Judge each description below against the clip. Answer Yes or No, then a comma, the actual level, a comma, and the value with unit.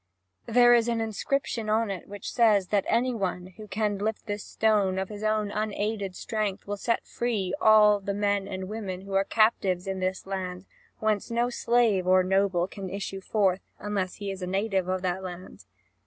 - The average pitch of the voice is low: No, high, 200 Hz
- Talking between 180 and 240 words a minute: Yes, average, 190 wpm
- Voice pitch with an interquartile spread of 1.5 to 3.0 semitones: Yes, narrow, 2.4 semitones